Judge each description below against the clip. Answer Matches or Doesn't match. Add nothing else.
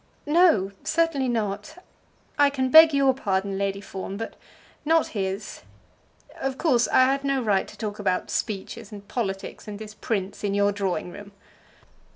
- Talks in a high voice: Matches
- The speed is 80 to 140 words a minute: Doesn't match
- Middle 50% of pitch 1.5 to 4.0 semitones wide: Doesn't match